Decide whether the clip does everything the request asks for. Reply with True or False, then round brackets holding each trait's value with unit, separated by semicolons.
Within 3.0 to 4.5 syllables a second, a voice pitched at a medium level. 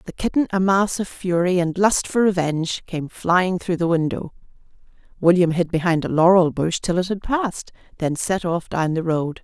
False (4.9 syllables/s; 175 Hz)